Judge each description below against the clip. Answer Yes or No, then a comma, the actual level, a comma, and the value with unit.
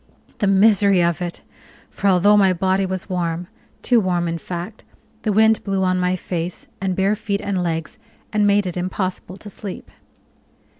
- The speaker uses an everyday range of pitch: No, narrow, 2.2 semitones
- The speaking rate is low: No, average, 170 wpm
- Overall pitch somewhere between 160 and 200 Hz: Yes, high, 190 Hz